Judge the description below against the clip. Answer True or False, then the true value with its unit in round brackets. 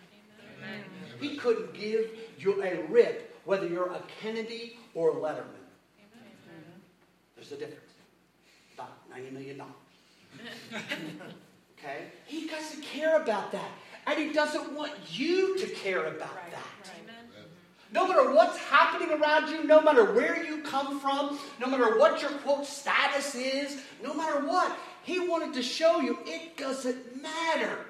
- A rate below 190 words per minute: True (140 wpm)